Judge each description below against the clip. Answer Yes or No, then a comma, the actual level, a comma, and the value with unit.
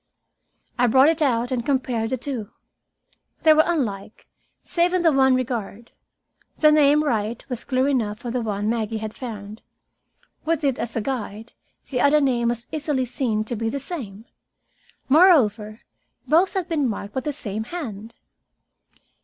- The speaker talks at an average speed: Yes, average, 160 wpm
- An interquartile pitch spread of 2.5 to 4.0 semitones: No, average, 4.6 semitones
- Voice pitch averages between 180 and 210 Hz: No, very high, 250 Hz